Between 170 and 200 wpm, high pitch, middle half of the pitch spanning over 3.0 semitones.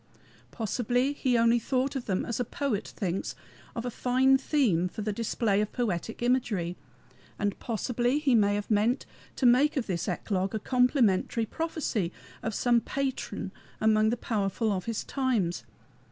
No: average, 160 wpm; high, 230 Hz; average, 3.7 semitones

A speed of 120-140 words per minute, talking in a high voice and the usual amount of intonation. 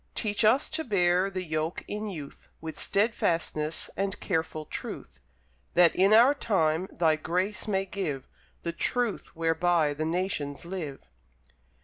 No: slow, 135 wpm; medium, 175 Hz; average, 3.9 semitones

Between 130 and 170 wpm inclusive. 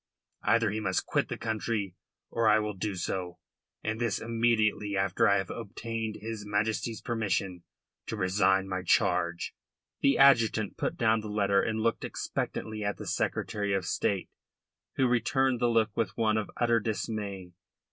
Yes: average, 160 wpm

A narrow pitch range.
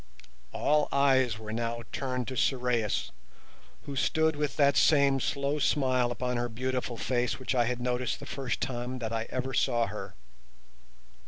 Yes: narrow, 2.2 semitones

